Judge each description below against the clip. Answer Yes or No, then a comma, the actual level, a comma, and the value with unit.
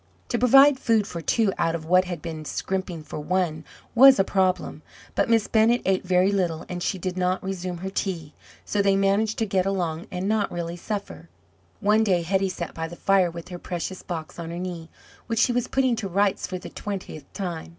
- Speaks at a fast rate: Yes, fast, 215 wpm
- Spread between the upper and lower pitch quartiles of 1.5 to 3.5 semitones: Yes, average, 2.9 semitones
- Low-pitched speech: No, medium, 185 Hz